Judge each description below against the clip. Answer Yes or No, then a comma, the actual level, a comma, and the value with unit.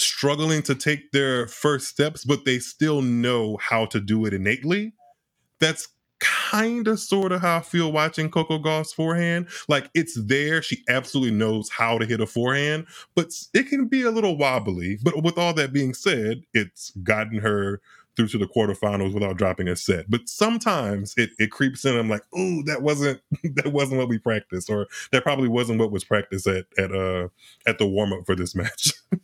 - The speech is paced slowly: No, average, 195 wpm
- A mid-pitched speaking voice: No, low, 130 Hz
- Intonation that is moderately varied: No, wide, 6.5 semitones